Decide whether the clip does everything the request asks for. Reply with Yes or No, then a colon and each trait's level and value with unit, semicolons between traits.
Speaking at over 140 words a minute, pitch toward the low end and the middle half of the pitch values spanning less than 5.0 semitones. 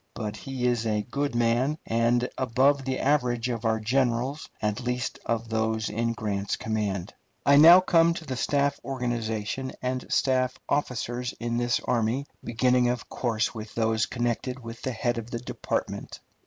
Yes: average, 165 wpm; low, 120 Hz; narrow, 2.5 semitones